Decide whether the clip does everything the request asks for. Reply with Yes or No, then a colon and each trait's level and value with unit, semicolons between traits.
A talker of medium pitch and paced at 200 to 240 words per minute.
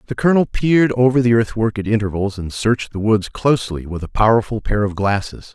No: low, 110 Hz; fast, 205 wpm